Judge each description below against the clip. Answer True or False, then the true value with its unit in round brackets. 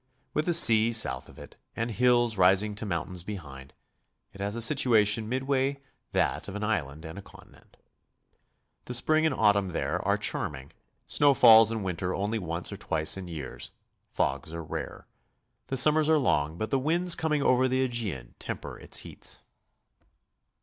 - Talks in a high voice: False (110 Hz)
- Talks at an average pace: True (170 wpm)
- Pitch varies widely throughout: True (6.1 semitones)